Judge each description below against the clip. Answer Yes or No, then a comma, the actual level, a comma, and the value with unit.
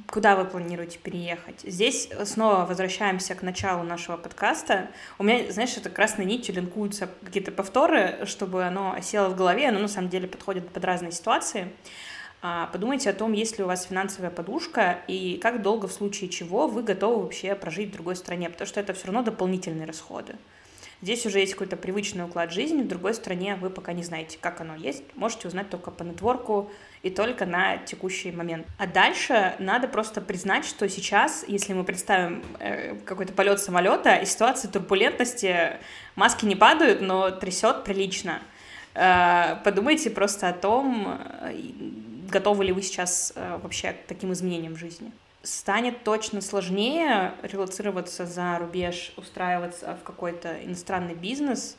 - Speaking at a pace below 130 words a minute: No, fast, 160 wpm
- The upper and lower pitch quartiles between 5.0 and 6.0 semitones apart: No, average, 2.9 semitones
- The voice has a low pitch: No, high, 195 Hz